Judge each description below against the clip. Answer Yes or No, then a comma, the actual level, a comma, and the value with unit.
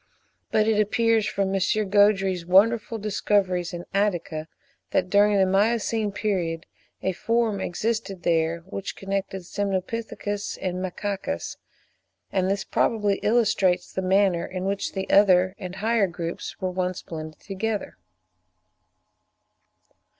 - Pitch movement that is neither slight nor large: No, narrow, 2.3 semitones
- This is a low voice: No, high, 195 Hz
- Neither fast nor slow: No, slow, 120 wpm